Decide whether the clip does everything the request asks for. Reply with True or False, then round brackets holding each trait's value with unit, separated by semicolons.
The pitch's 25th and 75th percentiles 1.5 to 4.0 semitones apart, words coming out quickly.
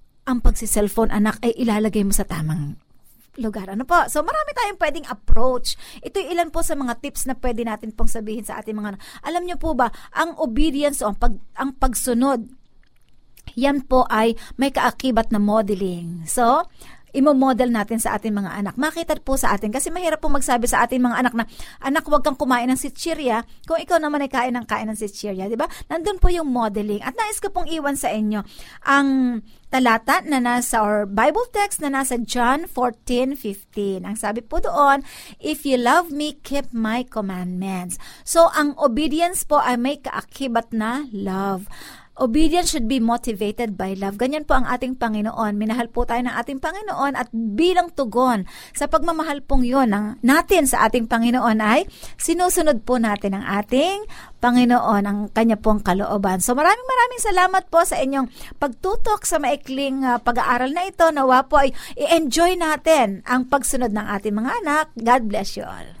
False (5.2 semitones; 180 wpm)